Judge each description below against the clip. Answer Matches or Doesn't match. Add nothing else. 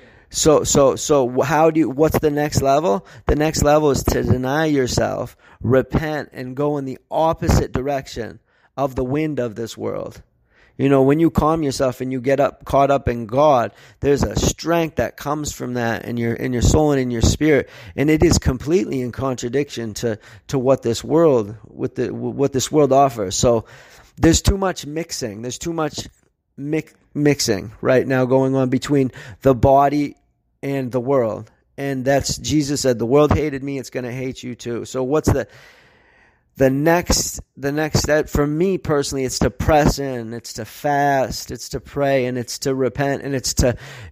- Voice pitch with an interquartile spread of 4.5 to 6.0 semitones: Doesn't match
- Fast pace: Doesn't match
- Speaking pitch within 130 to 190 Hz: Matches